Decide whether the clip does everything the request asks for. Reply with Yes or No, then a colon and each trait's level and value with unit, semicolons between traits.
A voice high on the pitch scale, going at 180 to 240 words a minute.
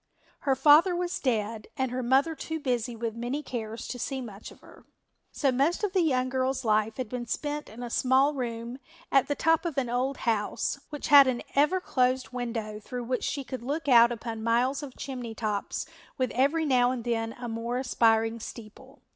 Yes: very high, 250 Hz; average, 200 wpm